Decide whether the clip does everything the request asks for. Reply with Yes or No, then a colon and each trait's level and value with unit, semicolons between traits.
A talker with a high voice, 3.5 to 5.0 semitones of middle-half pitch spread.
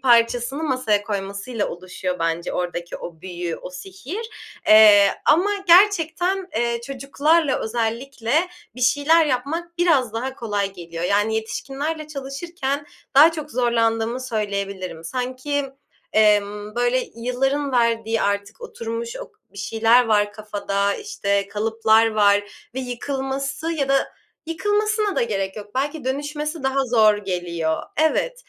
No: high, 235 Hz; wide, 5.6 semitones